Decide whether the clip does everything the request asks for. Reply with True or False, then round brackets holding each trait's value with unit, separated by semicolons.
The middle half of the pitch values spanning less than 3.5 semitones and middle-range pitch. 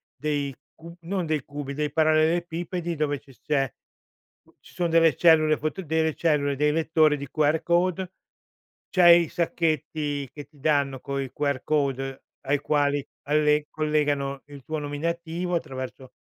True (2.4 semitones; 150 Hz)